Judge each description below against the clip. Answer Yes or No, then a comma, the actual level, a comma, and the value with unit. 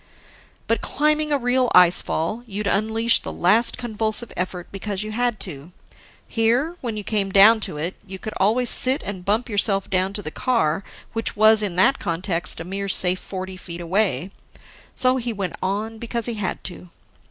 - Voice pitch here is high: Yes, high, 210 Hz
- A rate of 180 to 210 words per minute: Yes, average, 185 wpm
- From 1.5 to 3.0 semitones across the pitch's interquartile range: No, average, 3.7 semitones